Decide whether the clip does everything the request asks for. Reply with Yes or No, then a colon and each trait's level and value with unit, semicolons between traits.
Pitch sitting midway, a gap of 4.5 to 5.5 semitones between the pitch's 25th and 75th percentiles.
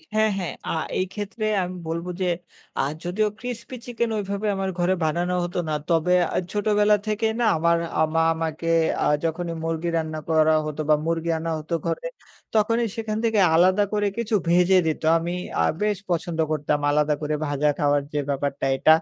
Yes: medium, 175 Hz; average, 4.8 semitones